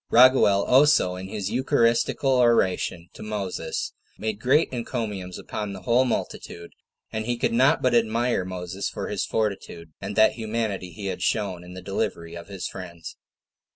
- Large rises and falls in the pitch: No, average, 4.3 semitones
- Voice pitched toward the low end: Yes, low, 105 Hz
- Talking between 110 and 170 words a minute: Yes, average, 160 wpm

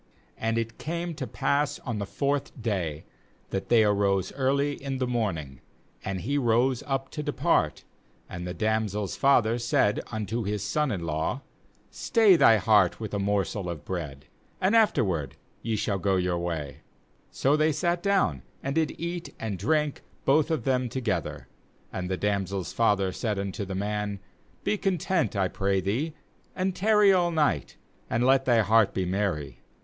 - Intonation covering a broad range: Yes, wide, 6.5 semitones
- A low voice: Yes, low, 110 Hz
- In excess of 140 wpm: Yes, average, 170 wpm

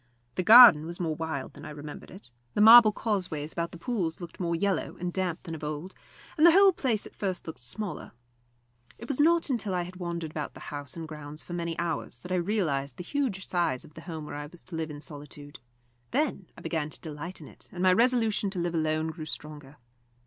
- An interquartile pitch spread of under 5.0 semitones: Yes, average, 4.6 semitones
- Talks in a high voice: No, medium, 170 Hz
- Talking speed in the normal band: No, fast, 230 wpm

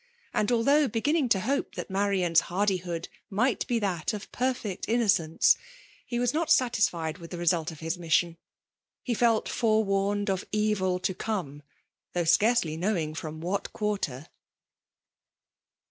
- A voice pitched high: Yes, high, 195 Hz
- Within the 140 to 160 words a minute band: Yes, average, 145 wpm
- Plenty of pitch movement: No, average, 4.9 semitones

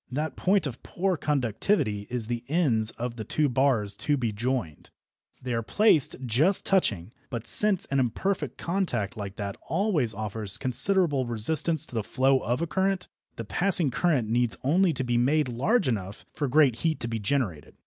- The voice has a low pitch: Yes, low, 130 Hz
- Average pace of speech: Yes, average, 180 wpm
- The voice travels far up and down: Yes, wide, 6.0 semitones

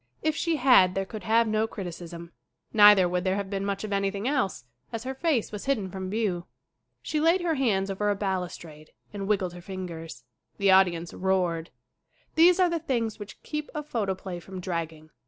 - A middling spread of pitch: Yes, average, 4.2 semitones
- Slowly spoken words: No, average, 190 wpm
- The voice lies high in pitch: Yes, high, 195 Hz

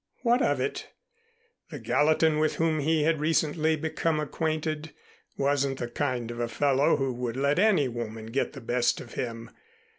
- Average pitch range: Yes, average, 4.3 semitones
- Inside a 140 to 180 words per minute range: Yes, average, 170 wpm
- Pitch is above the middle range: No, medium, 145 Hz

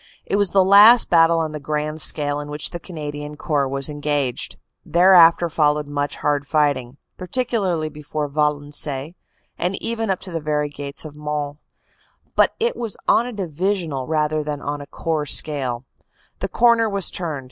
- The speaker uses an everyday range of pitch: Yes, average, 3.5 semitones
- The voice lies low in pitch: No, medium, 150 Hz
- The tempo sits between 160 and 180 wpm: Yes, average, 170 wpm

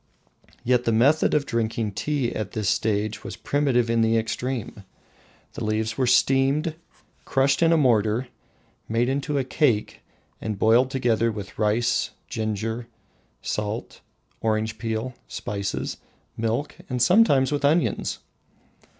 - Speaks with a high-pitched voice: No, low, 115 Hz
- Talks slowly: Yes, slow, 130 wpm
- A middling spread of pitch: Yes, average, 3.3 semitones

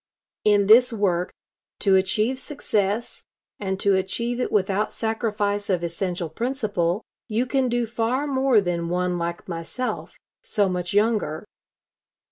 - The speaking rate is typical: No, slow, 130 wpm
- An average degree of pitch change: Yes, average, 4.5 semitones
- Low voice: No, high, 205 Hz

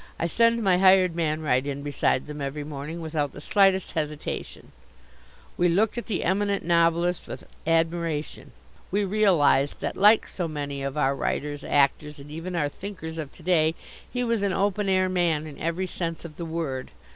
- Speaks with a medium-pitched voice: Yes, medium, 165 Hz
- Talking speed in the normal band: Yes, average, 180 wpm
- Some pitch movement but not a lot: Yes, average, 4.0 semitones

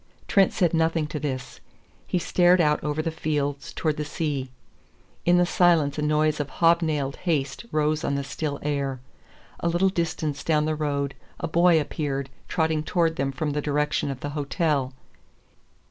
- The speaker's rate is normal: Yes, average, 170 wpm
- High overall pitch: No, medium, 150 Hz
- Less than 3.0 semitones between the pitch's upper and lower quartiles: Yes, narrow, 2.4 semitones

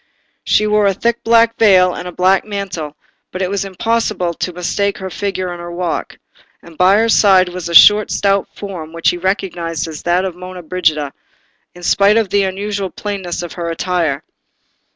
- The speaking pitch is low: No, medium, 185 Hz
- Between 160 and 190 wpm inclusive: Yes, average, 185 wpm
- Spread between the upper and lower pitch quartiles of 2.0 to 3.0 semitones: Yes, narrow, 2.5 semitones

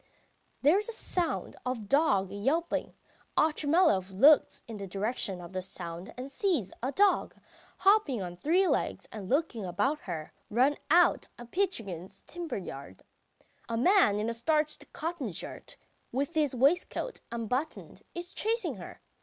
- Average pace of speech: Yes, average, 150 wpm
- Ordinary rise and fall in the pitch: No, wide, 8.7 semitones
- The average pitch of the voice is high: Yes, very high, 260 Hz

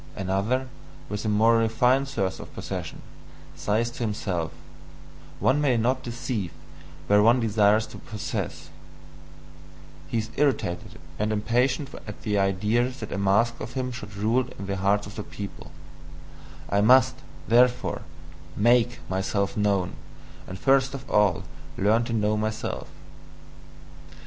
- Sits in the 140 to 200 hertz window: No, low, 110 Hz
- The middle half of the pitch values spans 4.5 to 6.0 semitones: No, average, 3.4 semitones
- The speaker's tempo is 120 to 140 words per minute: Yes, slow, 135 wpm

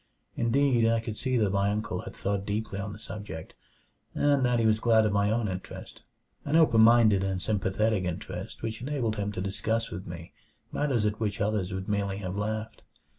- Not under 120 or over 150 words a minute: No, average, 195 wpm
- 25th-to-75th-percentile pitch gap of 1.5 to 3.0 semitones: Yes, narrow, 2.5 semitones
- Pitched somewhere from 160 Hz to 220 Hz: No, low, 105 Hz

